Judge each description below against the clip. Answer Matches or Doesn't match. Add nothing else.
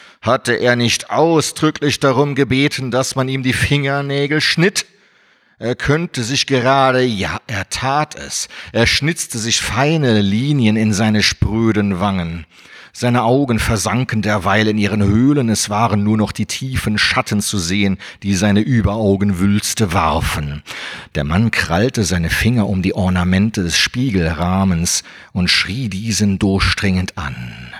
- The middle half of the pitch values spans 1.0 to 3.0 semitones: Doesn't match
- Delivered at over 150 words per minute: Doesn't match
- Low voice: Matches